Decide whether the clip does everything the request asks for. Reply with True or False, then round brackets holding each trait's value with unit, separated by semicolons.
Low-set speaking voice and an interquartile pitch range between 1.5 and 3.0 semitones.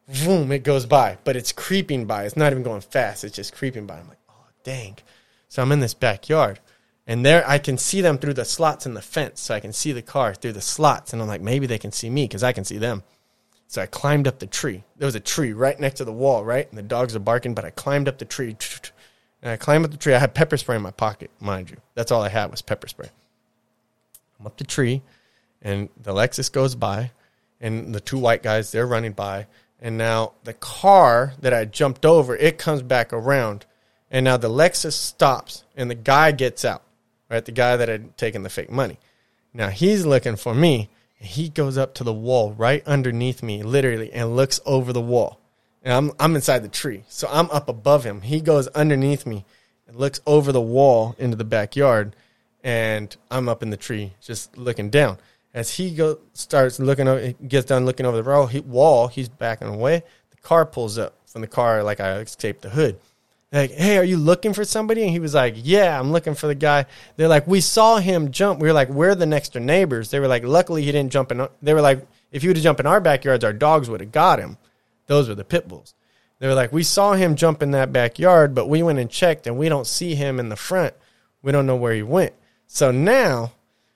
False (130 Hz; 4.4 semitones)